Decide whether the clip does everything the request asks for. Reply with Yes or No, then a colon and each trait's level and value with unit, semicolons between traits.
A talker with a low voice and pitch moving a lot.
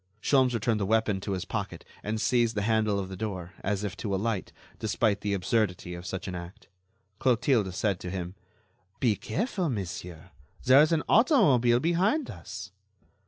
No: low, 105 Hz; average, 4.5 semitones